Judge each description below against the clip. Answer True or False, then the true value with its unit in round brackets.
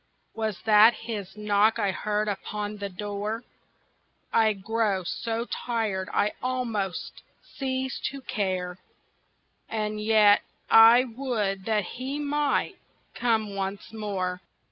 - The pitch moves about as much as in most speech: False (2.3 semitones)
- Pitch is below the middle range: False (215 Hz)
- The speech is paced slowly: True (115 wpm)